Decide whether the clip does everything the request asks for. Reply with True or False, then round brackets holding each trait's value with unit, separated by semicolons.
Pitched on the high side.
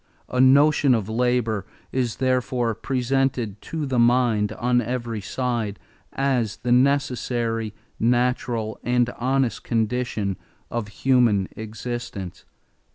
False (120 Hz)